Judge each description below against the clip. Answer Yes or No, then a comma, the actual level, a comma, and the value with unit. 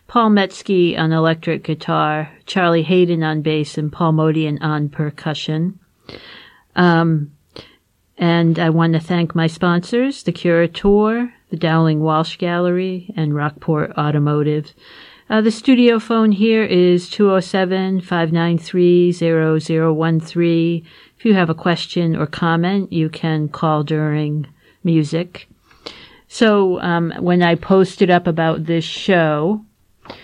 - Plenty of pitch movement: No, narrow, 2.6 semitones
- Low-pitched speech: No, medium, 170 Hz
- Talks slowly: Yes, slow, 115 wpm